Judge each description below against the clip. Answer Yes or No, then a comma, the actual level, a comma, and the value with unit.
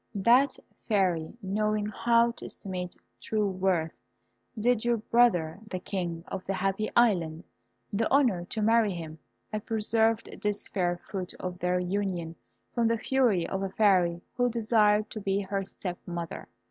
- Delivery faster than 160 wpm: No, average, 155 wpm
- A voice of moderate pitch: No, high, 200 Hz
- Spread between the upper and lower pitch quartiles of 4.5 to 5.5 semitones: No, average, 3.7 semitones